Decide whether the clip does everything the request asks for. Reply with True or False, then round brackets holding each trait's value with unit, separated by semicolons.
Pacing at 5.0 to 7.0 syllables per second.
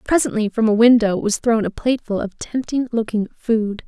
True (5.2 syllables/s)